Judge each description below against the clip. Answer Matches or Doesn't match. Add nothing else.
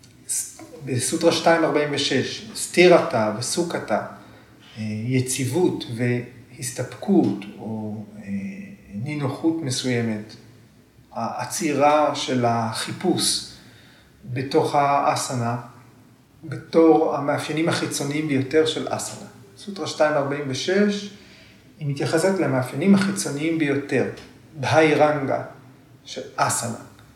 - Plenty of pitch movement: Doesn't match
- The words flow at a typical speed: Doesn't match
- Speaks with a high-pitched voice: Doesn't match